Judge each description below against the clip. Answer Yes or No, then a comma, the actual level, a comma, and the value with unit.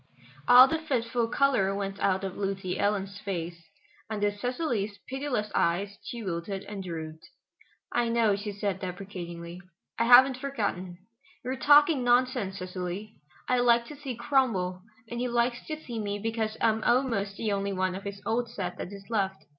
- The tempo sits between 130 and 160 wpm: No, average, 170 wpm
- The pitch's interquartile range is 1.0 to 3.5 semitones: No, average, 4.0 semitones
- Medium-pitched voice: No, high, 205 Hz